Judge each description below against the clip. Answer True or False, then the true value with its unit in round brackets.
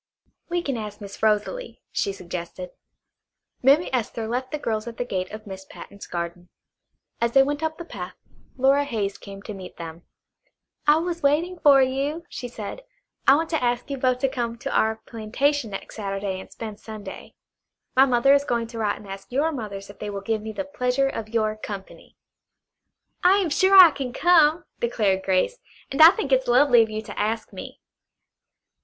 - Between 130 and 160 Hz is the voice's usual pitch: False (235 Hz)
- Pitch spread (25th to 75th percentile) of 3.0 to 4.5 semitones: False (5.6 semitones)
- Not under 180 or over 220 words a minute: True (195 wpm)